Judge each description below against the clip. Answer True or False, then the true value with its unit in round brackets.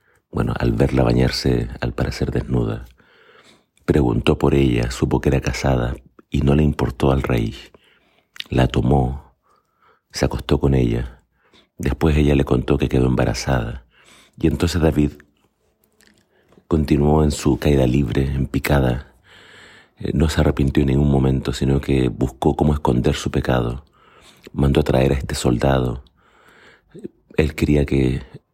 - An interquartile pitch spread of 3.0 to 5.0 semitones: False (2.4 semitones)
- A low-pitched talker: True (70 Hz)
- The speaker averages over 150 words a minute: False (135 wpm)